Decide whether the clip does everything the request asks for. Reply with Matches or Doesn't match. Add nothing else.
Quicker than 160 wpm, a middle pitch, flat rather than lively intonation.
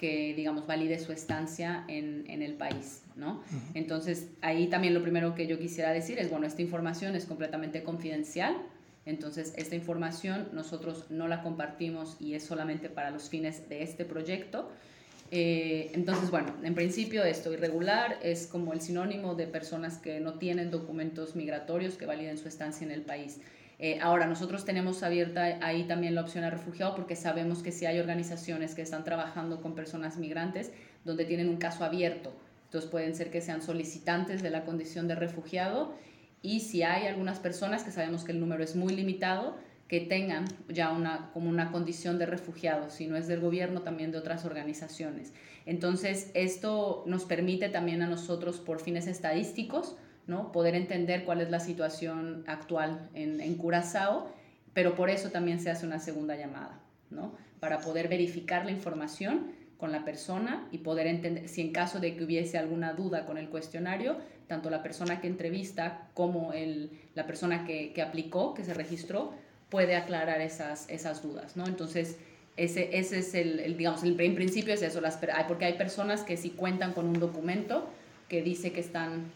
Matches